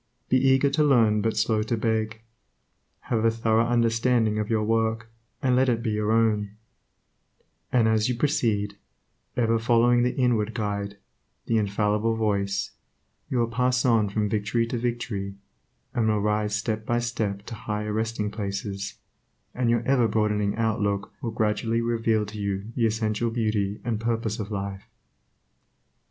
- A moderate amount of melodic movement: No, narrow, 1.8 semitones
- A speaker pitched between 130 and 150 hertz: No, low, 110 Hz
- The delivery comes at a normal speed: Yes, average, 155 wpm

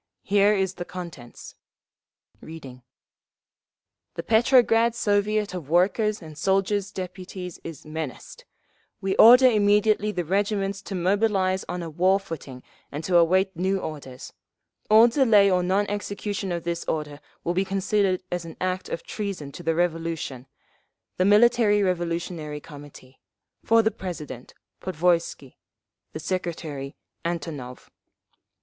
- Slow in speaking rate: Yes, slow, 130 wpm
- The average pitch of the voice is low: No, medium, 185 Hz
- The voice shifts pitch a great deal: No, average, 3.8 semitones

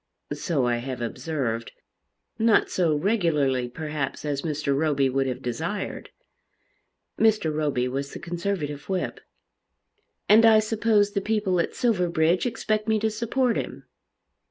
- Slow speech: Yes, slow, 130 wpm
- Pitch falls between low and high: Yes, medium, 165 Hz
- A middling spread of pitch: No, wide, 7.3 semitones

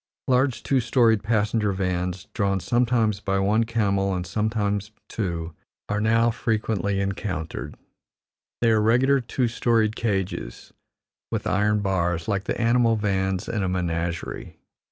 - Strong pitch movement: No, average, 3.1 semitones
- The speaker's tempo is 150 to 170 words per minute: No, slow, 135 wpm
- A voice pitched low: Yes, low, 105 Hz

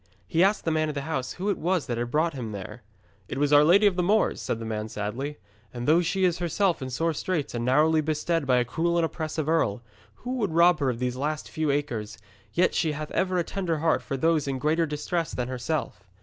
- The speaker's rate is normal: No, fast, 245 wpm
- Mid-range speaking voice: Yes, medium, 155 Hz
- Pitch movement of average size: Yes, average, 4.7 semitones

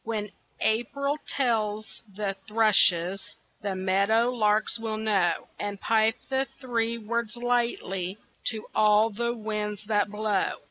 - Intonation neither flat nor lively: No, narrow, 2.1 semitones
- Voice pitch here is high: Yes, high, 215 Hz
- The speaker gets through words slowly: Yes, slow, 125 wpm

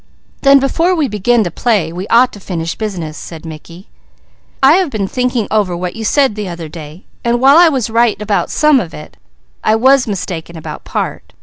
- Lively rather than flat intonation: Yes, wide, 6.7 semitones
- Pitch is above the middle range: Yes, high, 215 Hz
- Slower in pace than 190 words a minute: No, average, 200 wpm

